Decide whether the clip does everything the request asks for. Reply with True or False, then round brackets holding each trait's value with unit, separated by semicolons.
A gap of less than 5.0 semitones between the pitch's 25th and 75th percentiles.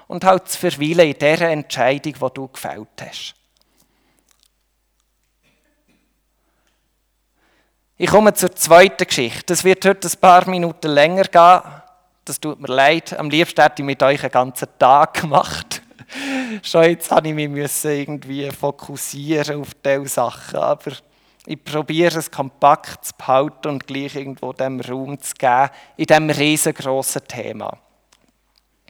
True (3.9 semitones)